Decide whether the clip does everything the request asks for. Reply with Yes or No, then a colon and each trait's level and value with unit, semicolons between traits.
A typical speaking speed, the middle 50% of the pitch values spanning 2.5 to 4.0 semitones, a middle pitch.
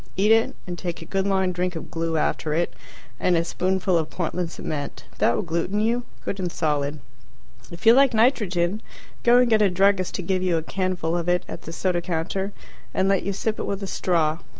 No: fast, 220 wpm; average, 2.8 semitones; medium, 180 Hz